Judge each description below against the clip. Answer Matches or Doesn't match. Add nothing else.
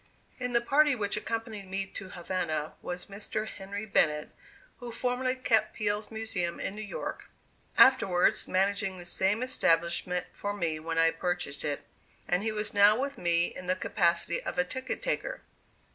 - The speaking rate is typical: Matches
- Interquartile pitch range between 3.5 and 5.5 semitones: Matches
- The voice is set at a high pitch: Matches